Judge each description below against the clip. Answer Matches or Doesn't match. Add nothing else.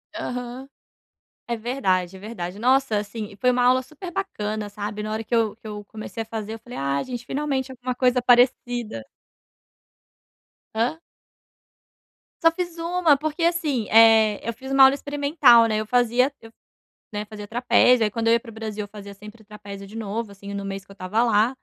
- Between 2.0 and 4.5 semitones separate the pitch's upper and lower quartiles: Matches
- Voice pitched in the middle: Doesn't match